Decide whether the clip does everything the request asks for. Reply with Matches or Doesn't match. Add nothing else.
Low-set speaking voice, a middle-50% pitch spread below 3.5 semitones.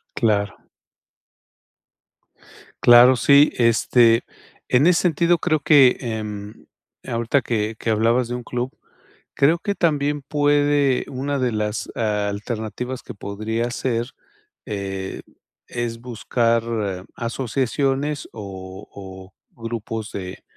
Doesn't match